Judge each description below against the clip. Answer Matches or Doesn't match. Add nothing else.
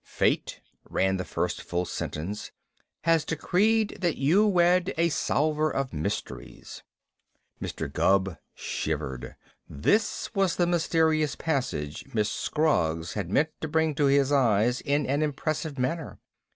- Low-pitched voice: Doesn't match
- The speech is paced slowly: Matches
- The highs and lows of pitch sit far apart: Matches